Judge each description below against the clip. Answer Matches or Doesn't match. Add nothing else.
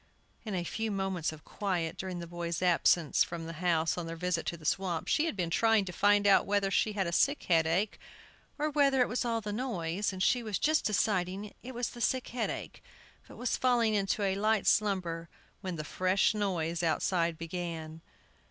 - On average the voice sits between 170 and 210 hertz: Matches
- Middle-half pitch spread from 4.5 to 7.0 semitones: Doesn't match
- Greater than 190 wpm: Matches